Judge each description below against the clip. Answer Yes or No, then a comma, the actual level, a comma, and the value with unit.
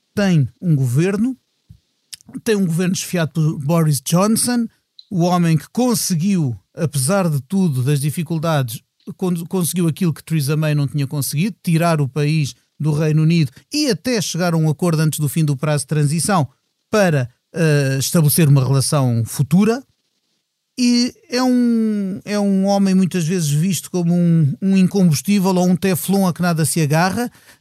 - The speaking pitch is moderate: Yes, medium, 170 Hz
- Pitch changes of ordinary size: Yes, average, 4.3 semitones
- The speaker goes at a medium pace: Yes, average, 160 wpm